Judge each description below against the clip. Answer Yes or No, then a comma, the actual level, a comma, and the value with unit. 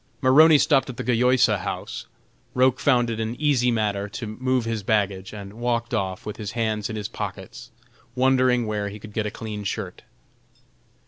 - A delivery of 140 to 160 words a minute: No, average, 180 wpm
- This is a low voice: Yes, low, 115 Hz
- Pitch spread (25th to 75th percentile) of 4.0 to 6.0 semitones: No, average, 3.2 semitones